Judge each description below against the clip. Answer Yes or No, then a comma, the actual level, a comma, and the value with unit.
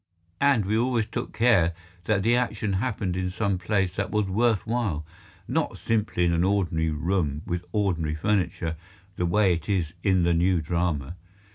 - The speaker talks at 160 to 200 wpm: Yes, average, 170 wpm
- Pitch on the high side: No, very low, 95 Hz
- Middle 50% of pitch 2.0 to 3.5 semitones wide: No, average, 3.9 semitones